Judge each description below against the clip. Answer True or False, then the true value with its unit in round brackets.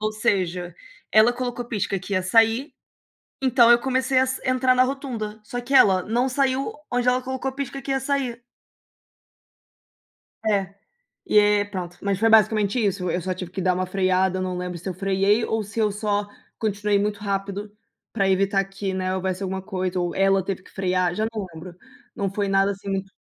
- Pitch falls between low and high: False (205 Hz)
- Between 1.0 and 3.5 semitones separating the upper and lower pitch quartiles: False (4.0 semitones)